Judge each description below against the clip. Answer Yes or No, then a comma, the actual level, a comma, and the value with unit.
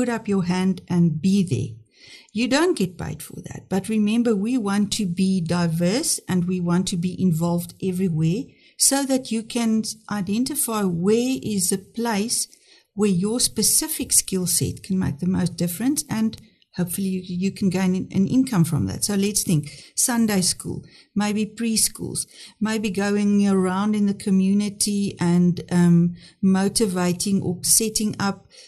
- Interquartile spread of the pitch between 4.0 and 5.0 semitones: No, average, 3.6 semitones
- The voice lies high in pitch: Yes, high, 195 Hz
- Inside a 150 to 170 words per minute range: Yes, average, 155 wpm